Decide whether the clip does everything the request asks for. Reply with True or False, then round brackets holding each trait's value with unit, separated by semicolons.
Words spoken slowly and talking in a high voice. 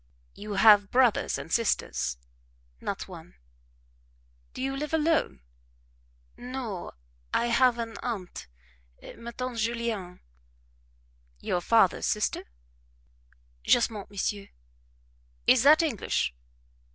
True (95 wpm; 230 Hz)